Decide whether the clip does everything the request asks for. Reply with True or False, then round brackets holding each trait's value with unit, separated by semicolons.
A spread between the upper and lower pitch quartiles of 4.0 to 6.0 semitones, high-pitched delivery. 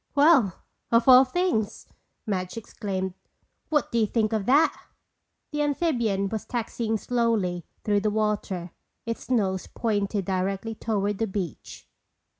False (3.3 semitones; 215 Hz)